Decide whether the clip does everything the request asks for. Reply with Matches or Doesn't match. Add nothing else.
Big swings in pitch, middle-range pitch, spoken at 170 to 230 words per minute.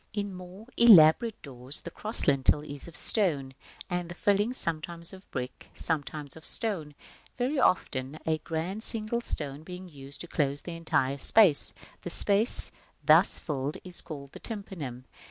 Doesn't match